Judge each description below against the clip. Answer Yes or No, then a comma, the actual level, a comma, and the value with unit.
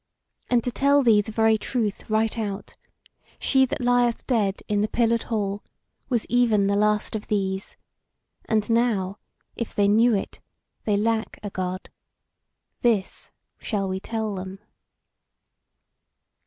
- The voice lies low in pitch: No, high, 215 Hz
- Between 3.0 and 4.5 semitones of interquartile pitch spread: No, narrow, 2.5 semitones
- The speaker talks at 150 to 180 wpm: No, average, 140 wpm